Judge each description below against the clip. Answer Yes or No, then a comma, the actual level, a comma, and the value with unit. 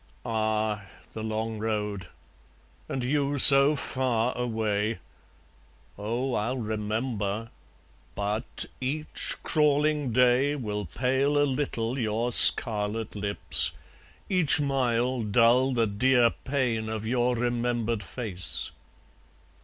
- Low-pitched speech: Yes, low, 115 Hz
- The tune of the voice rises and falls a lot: No, average, 3.4 semitones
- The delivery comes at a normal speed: No, slow, 100 wpm